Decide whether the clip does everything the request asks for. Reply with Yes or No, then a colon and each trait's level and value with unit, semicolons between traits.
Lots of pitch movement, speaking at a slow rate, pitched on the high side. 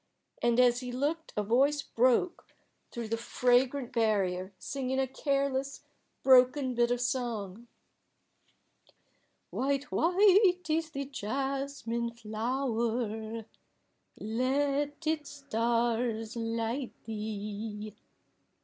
No: average, 3.5 semitones; slow, 95 wpm; high, 245 Hz